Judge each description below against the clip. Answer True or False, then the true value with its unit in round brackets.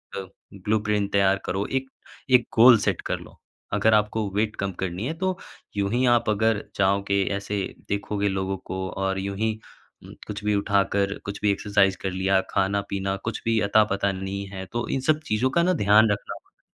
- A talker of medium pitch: False (100 Hz)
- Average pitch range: False (2.1 semitones)